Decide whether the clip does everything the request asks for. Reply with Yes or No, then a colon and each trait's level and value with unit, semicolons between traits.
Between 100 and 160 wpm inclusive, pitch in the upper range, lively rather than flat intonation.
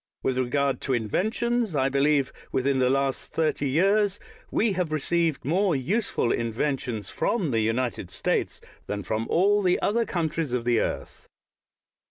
No: average, 150 wpm; medium, 140 Hz; wide, 6.5 semitones